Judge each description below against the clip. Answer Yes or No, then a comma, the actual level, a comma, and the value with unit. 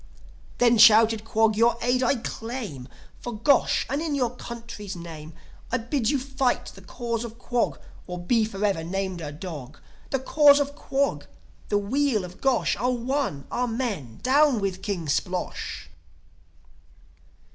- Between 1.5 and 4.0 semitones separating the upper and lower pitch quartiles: No, average, 4.8 semitones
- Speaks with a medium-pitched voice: No, high, 230 Hz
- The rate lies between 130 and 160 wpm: Yes, average, 150 wpm